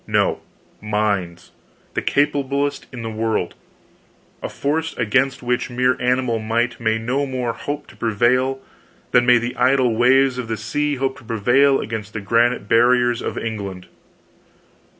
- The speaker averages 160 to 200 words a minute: No, average, 145 wpm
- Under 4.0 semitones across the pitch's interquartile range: Yes, average, 2.9 semitones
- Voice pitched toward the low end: Yes, low, 120 Hz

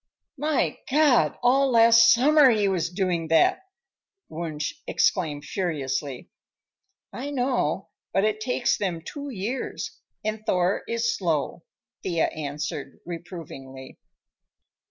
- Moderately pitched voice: No, high, 195 Hz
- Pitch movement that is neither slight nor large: No, wide, 7.2 semitones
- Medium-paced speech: No, slow, 110 wpm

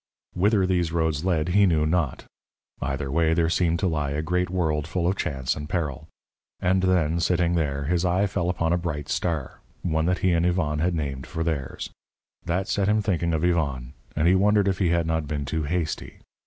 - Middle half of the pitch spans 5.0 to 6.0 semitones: No, average, 2.9 semitones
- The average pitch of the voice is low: Yes, very low, 85 Hz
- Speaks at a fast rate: Yes, fast, 210 wpm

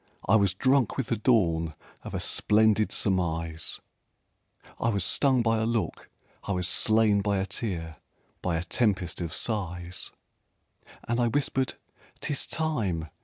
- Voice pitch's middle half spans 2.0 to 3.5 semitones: No, average, 4.7 semitones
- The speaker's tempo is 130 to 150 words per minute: Yes, average, 145 wpm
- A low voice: Yes, low, 100 Hz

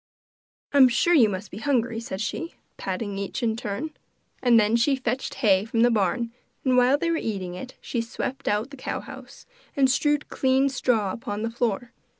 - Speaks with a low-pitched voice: No, high, 235 Hz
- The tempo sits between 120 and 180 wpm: No, average, 190 wpm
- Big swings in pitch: No, average, 4.0 semitones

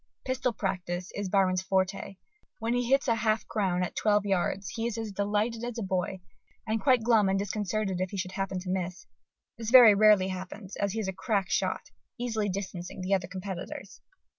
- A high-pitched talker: Yes, high, 200 Hz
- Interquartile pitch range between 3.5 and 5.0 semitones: No, average, 2.9 semitones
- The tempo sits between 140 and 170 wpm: No, average, 195 wpm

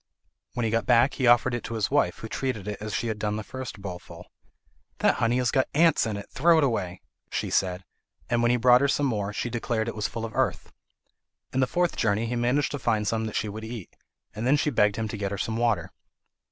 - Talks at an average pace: No, fast, 250 wpm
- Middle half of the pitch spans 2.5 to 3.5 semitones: Yes, average, 2.9 semitones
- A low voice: Yes, low, 115 Hz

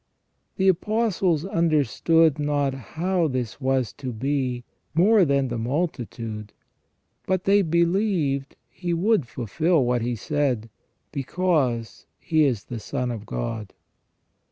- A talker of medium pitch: Yes, medium, 145 Hz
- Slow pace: Yes, slow, 125 wpm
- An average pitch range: No, wide, 5.7 semitones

